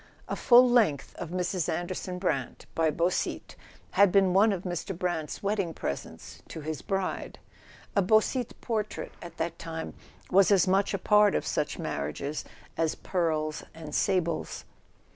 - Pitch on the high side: No, medium, 180 Hz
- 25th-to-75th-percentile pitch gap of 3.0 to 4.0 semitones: Yes, average, 3.5 semitones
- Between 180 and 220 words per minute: No, average, 150 wpm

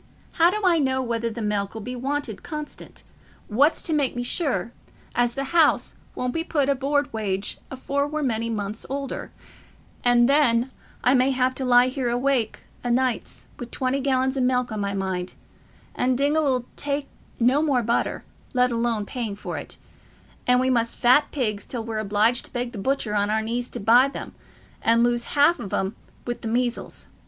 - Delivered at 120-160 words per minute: No, average, 185 wpm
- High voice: Yes, high, 245 Hz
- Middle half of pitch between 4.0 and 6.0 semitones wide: No, average, 3.1 semitones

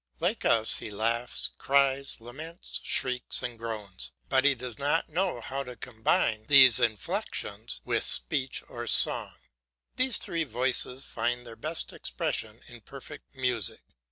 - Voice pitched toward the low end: Yes, low, 125 Hz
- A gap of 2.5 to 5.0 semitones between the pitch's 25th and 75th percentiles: Yes, average, 3.2 semitones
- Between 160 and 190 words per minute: No, average, 140 wpm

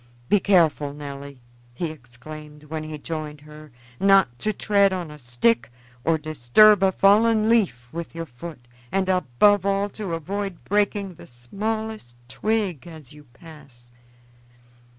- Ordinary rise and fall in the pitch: No, wide, 5.8 semitones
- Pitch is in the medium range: Yes, medium, 160 Hz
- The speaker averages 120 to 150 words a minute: Yes, average, 140 wpm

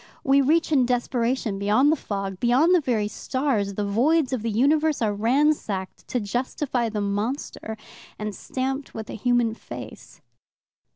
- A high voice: Yes, high, 245 Hz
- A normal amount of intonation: Yes, average, 4.5 semitones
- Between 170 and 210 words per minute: No, average, 155 wpm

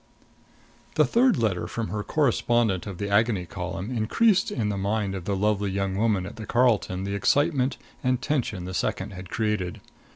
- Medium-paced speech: Yes, average, 175 wpm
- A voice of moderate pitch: No, low, 105 Hz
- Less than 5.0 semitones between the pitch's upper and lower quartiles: Yes, average, 3.8 semitones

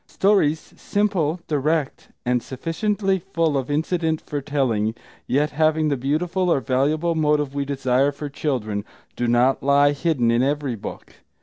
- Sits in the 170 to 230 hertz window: No, medium, 145 Hz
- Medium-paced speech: Yes, average, 145 wpm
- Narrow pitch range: No, average, 3.3 semitones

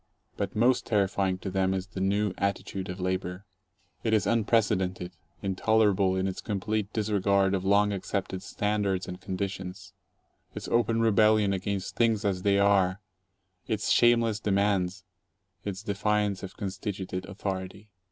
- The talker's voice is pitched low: Yes, low, 100 Hz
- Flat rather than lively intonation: Yes, narrow, 2.0 semitones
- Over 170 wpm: No, slow, 135 wpm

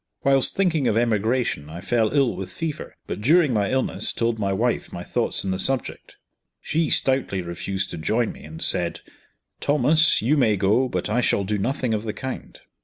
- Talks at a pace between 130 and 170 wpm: No, average, 190 wpm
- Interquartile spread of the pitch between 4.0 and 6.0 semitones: Yes, wide, 5.4 semitones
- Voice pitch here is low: Yes, low, 115 Hz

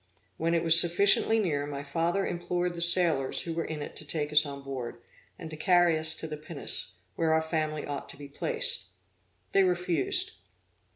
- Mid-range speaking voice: Yes, medium, 160 Hz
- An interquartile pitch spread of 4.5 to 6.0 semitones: No, average, 2.9 semitones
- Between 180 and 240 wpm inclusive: Yes, average, 190 wpm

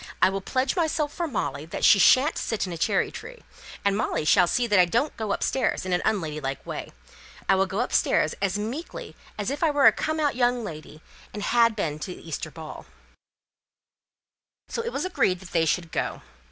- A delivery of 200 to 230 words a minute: Yes, fast, 205 wpm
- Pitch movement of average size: No, wide, 7.2 semitones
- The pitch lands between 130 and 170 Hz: No, high, 205 Hz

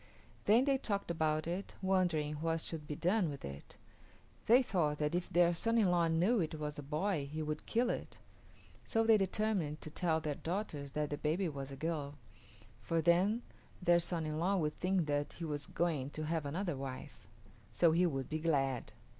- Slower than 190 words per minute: No, average, 195 wpm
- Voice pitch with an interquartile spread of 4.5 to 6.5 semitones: No, average, 3.6 semitones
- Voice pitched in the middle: Yes, medium, 165 Hz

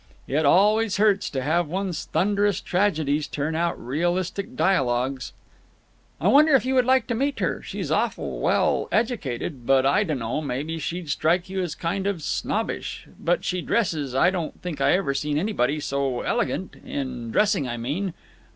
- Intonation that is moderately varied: No, wide, 6.1 semitones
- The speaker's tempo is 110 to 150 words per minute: No, average, 165 wpm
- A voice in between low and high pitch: Yes, medium, 170 Hz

